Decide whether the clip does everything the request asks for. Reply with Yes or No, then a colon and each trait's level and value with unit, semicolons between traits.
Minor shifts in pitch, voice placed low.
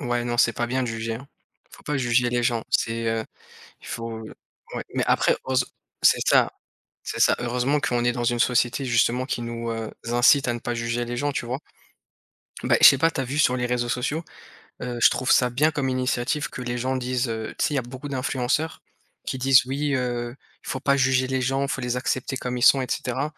Yes: narrow, 1.8 semitones; low, 125 Hz